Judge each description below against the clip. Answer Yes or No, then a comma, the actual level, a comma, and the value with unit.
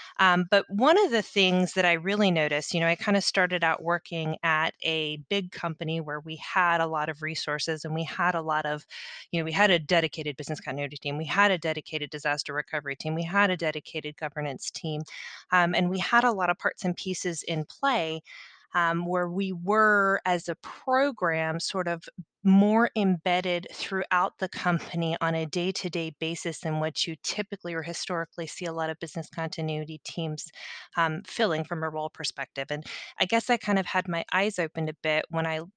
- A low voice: No, medium, 170 Hz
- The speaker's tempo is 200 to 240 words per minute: Yes, fast, 205 wpm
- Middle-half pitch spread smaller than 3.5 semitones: Yes, average, 2.8 semitones